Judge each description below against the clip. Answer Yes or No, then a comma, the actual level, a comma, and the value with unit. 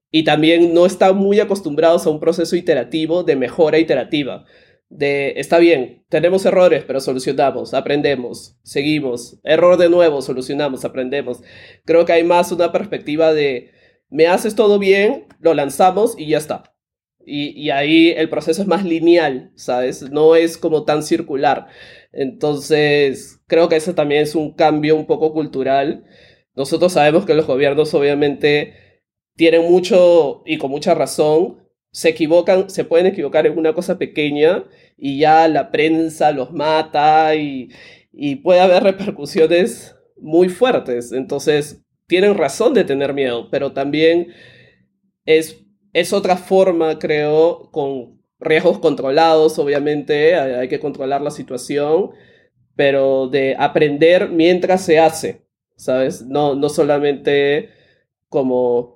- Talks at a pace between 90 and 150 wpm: Yes, average, 140 wpm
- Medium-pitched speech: Yes, medium, 155 Hz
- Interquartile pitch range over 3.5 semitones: No, average, 3.2 semitones